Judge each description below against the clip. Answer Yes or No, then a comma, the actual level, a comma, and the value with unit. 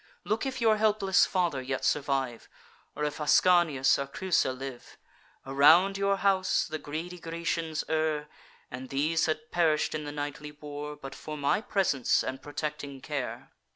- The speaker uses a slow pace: No, average, 155 wpm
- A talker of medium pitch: Yes, medium, 150 Hz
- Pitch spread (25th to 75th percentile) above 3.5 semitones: Yes, average, 4.0 semitones